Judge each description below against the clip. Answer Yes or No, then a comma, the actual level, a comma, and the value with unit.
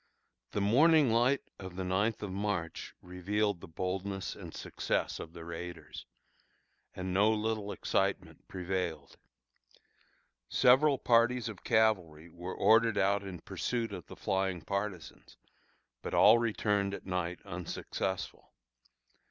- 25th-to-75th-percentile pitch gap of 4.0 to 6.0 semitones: No, average, 3.5 semitones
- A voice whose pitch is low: Yes, low, 100 Hz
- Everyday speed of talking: No, slow, 125 wpm